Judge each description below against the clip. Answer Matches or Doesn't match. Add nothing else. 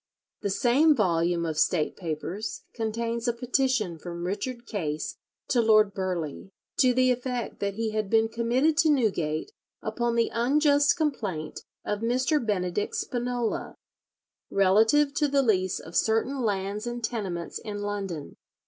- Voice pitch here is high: Matches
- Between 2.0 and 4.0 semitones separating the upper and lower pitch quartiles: Doesn't match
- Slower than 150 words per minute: Matches